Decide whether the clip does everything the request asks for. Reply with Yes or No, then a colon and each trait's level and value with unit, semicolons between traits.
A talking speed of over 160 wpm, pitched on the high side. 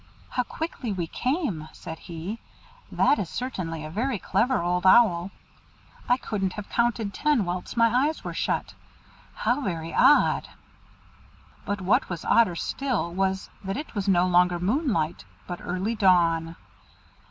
No: average, 145 wpm; high, 195 Hz